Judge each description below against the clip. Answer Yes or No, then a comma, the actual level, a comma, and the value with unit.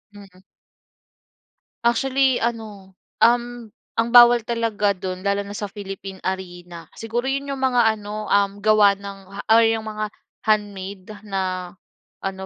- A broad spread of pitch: No, average, 3.0 semitones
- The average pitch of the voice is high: Yes, high, 210 Hz